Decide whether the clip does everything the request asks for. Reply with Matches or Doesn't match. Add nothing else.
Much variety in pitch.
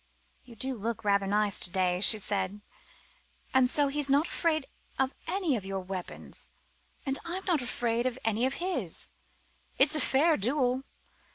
Matches